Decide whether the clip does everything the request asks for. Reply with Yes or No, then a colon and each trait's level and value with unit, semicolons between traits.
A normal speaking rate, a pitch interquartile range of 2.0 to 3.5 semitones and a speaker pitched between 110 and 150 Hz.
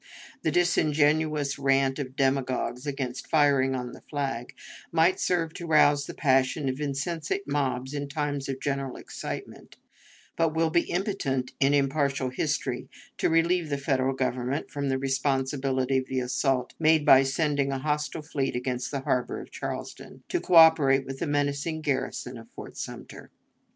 Yes: average, 155 wpm; narrow, 2.5 semitones; medium, 140 Hz